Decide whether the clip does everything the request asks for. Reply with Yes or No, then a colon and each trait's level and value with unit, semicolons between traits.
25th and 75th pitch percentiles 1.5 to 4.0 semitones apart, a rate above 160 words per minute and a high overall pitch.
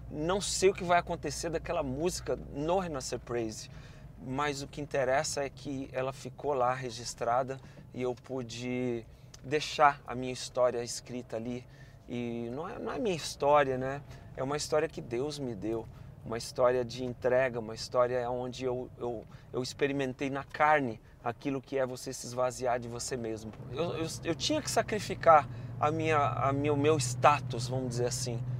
No: average, 2.8 semitones; average, 170 wpm; low, 130 Hz